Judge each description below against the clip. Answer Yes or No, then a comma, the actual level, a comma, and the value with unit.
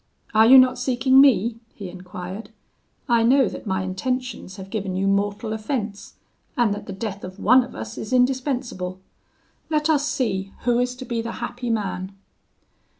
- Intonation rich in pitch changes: No, average, 4.6 semitones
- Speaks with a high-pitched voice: Yes, high, 225 Hz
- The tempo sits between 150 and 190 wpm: Yes, average, 170 wpm